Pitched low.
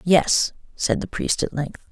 No: medium, 160 Hz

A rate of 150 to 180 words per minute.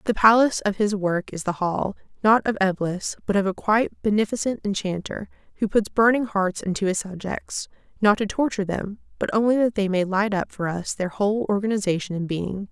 No: average, 200 wpm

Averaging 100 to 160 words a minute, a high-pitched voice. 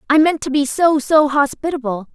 Yes: average, 140 wpm; very high, 290 Hz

